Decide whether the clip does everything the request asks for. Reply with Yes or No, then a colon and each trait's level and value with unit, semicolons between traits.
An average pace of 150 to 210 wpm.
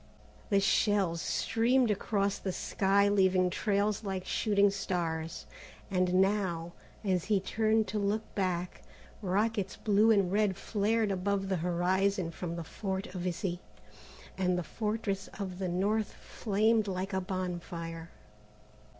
No: slow, 135 wpm